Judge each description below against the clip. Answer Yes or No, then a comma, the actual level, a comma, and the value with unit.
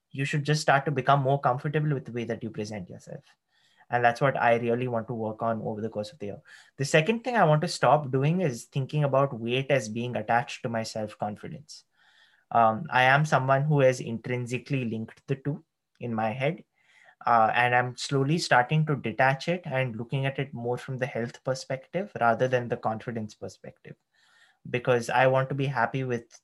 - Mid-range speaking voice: No, low, 130 Hz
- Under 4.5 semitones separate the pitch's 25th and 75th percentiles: Yes, average, 3.3 semitones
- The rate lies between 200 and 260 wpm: Yes, fast, 205 wpm